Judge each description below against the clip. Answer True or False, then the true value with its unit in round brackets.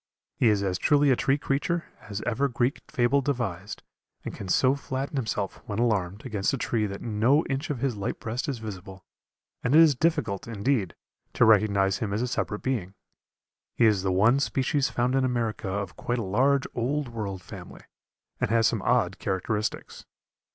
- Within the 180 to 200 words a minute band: True (185 wpm)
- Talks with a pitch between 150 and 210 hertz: False (115 Hz)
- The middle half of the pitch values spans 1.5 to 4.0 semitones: False (4.9 semitones)